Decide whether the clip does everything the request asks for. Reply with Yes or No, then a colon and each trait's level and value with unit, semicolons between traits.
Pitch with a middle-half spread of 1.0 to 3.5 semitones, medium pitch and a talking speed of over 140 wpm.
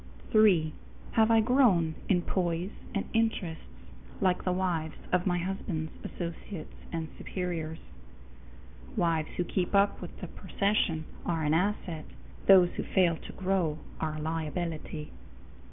No: average, 3.2 semitones; medium, 175 Hz; slow, 135 wpm